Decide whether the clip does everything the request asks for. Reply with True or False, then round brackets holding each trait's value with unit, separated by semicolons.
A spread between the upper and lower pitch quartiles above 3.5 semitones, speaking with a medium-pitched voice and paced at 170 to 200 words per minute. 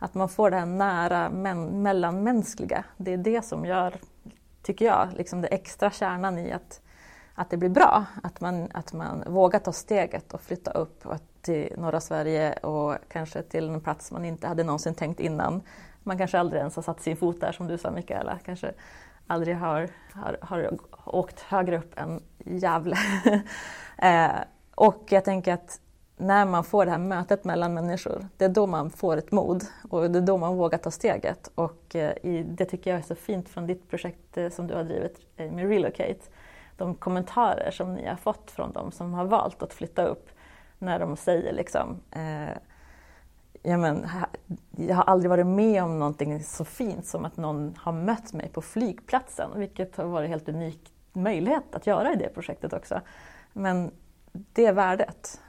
False (2.7 semitones; 180 Hz; 185 wpm)